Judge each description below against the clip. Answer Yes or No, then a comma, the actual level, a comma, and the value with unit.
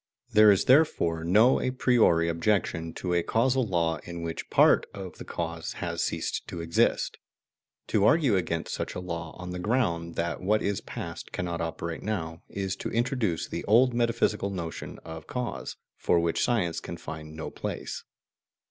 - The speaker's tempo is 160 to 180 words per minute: Yes, average, 170 wpm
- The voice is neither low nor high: No, very low, 90 Hz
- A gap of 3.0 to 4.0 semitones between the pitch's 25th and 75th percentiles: No, average, 5.0 semitones